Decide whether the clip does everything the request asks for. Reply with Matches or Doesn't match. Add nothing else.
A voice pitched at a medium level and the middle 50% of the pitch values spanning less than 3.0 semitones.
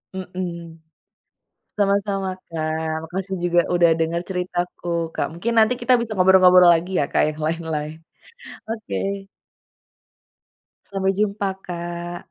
Matches